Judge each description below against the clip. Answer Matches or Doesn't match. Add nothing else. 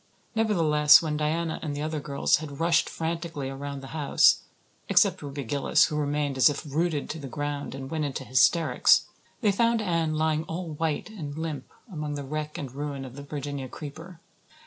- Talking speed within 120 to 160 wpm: Doesn't match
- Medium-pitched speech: Matches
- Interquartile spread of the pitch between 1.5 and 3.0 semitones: Matches